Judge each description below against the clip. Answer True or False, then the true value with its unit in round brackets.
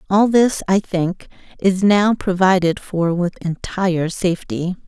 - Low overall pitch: False (185 Hz)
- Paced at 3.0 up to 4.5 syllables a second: True (4.2 syllables/s)